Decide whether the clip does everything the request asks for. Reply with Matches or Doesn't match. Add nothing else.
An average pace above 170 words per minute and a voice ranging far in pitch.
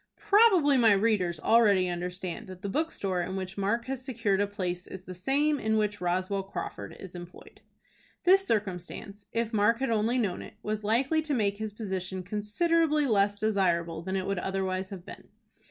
Doesn't match